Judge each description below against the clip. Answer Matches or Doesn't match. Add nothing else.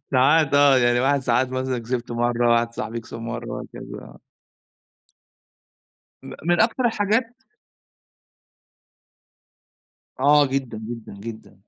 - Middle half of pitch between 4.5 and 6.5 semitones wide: Doesn't match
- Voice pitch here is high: Doesn't match